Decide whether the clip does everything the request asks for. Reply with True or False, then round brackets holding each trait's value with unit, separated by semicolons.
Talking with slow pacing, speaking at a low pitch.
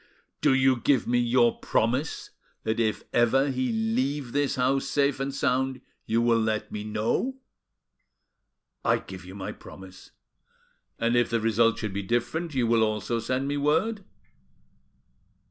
False (150 wpm; 120 Hz)